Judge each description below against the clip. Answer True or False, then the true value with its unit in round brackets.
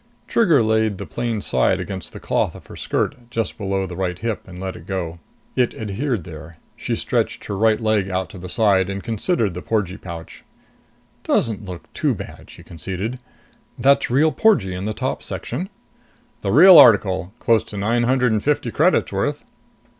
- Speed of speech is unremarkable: True (180 wpm)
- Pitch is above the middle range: False (105 Hz)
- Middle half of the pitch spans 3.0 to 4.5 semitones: True (4.0 semitones)